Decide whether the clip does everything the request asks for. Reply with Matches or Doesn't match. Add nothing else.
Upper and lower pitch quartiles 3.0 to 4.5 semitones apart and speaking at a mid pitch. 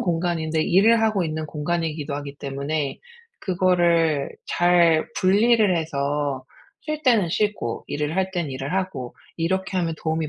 Matches